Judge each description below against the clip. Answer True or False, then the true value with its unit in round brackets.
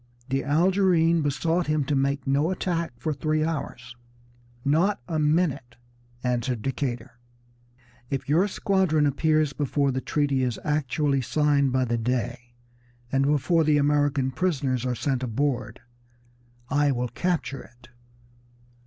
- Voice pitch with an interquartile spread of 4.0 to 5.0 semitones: False (3.2 semitones)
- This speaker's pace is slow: True (130 wpm)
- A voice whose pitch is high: False (140 Hz)